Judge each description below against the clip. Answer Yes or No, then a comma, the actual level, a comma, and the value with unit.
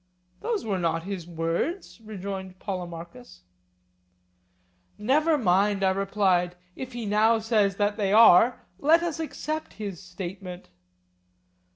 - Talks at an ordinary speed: No, slow, 115 wpm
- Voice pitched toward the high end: Yes, high, 200 Hz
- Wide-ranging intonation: No, average, 4.0 semitones